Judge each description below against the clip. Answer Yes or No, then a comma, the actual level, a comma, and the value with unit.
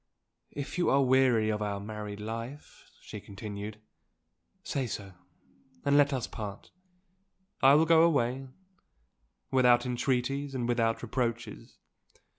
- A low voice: Yes, low, 120 Hz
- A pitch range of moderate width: Yes, average, 4.0 semitones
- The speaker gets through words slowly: Yes, slow, 120 wpm